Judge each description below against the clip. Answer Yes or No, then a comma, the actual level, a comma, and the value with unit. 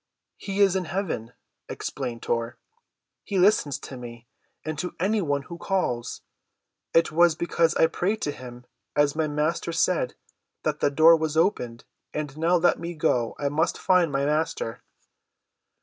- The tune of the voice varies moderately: Yes, average, 4.1 semitones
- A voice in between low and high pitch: Yes, medium, 155 Hz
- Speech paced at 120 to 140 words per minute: No, average, 160 wpm